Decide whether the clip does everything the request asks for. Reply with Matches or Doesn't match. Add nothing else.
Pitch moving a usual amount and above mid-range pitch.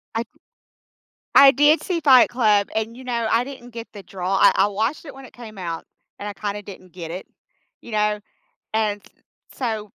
Matches